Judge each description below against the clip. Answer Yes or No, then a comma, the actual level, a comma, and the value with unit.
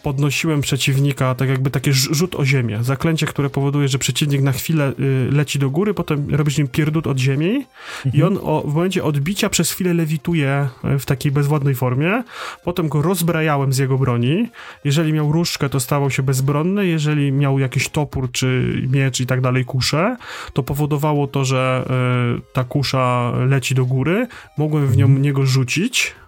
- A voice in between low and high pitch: Yes, medium, 145 Hz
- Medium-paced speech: No, fast, 165 wpm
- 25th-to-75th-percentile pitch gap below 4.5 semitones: Yes, average, 2.8 semitones